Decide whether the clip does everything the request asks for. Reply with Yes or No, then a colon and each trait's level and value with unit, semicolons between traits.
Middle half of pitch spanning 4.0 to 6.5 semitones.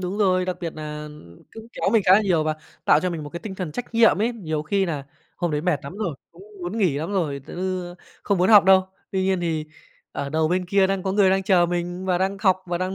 No: average, 3.0 semitones